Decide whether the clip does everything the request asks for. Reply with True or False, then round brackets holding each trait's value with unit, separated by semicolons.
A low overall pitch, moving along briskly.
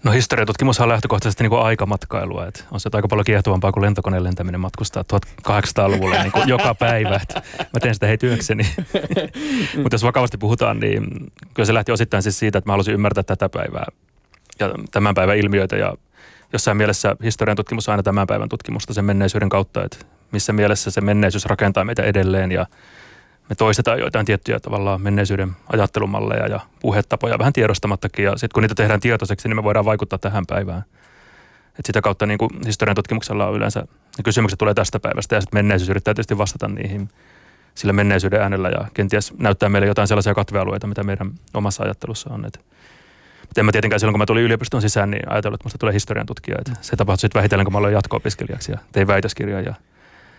True (105 Hz; 185 wpm)